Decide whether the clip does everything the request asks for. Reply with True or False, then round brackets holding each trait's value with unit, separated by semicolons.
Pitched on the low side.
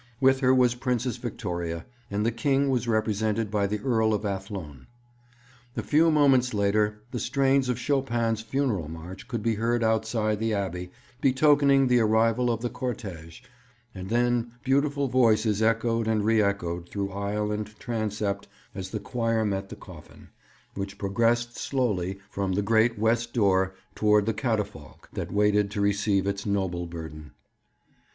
True (110 Hz)